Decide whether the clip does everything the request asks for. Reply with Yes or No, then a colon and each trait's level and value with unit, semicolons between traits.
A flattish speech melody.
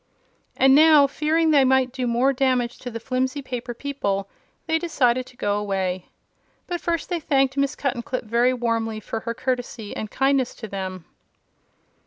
No: average, 3.3 semitones